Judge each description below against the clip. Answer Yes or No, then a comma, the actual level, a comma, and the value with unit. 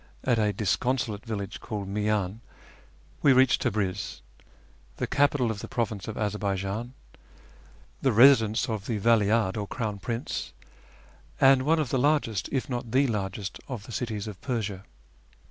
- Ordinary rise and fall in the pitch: Yes, average, 3.4 semitones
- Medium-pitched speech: No, low, 110 Hz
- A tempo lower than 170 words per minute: Yes, average, 150 wpm